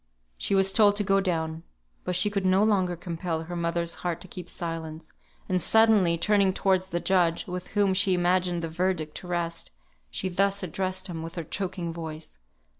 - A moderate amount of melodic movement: No, narrow, 2.3 semitones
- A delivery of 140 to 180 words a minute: No, average, 190 wpm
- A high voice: No, medium, 180 Hz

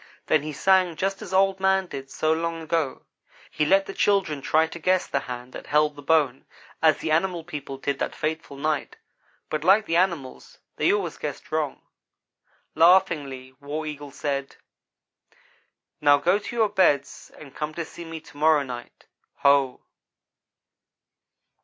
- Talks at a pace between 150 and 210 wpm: Yes, average, 160 wpm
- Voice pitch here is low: No, medium, 155 Hz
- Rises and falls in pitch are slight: No, average, 3.9 semitones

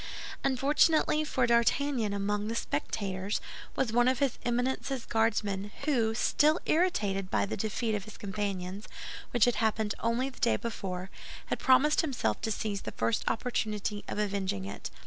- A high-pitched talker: Yes, high, 220 Hz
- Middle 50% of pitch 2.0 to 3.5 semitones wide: No, average, 4.1 semitones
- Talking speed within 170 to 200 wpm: No, average, 155 wpm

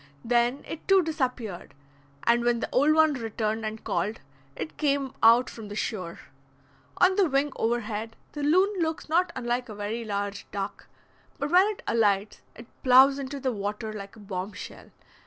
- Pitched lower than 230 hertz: No, high, 240 Hz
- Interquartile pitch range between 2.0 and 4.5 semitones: No, average, 5.1 semitones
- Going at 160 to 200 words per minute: Yes, average, 170 wpm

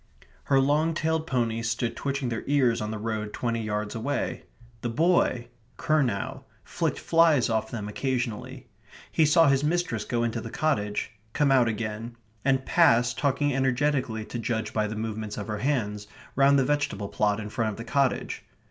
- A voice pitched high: No, low, 120 Hz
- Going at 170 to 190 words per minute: Yes, average, 175 wpm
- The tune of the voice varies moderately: Yes, average, 4.3 semitones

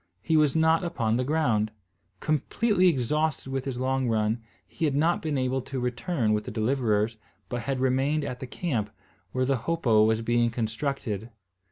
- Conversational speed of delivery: Yes, average, 175 wpm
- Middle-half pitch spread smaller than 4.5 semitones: No, average, 4.8 semitones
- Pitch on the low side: Yes, low, 130 Hz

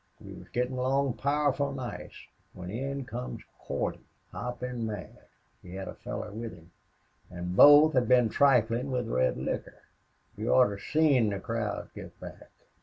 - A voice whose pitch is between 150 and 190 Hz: No, low, 125 Hz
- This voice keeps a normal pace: Yes, average, 155 wpm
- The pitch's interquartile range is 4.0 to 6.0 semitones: Yes, average, 4.5 semitones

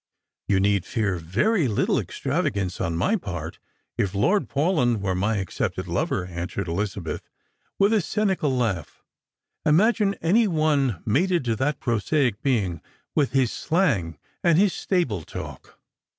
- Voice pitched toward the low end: Yes, low, 120 Hz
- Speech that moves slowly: No, average, 145 wpm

